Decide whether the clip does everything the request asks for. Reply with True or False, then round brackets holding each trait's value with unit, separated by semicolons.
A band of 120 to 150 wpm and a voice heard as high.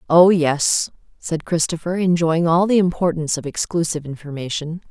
False (135 wpm; 165 Hz)